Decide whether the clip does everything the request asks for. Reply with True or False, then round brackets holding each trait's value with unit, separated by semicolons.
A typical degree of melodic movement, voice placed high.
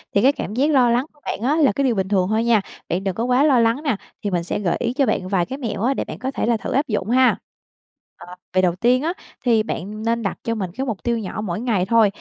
True (4.6 semitones; 230 Hz)